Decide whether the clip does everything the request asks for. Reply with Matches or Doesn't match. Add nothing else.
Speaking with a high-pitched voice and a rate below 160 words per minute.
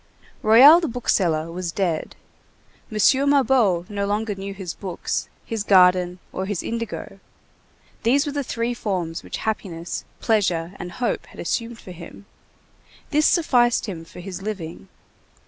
Matches